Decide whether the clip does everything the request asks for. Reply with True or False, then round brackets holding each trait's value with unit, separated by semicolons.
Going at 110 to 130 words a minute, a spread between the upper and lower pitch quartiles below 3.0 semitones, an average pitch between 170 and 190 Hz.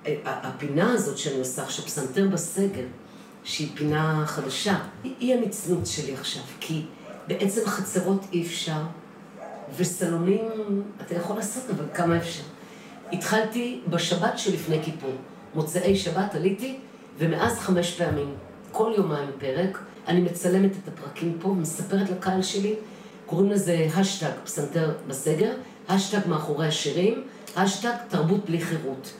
False (125 wpm; 4.5 semitones; 185 Hz)